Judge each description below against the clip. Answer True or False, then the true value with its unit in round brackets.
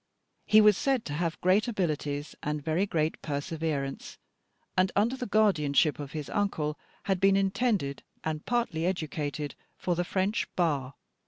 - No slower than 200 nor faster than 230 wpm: False (150 wpm)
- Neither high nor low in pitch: True (170 Hz)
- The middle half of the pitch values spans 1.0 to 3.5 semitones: False (4.9 semitones)